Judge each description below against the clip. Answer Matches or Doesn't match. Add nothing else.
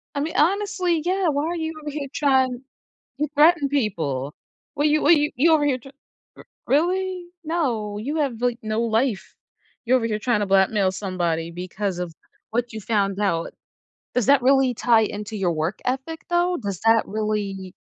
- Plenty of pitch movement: Matches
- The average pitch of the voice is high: Matches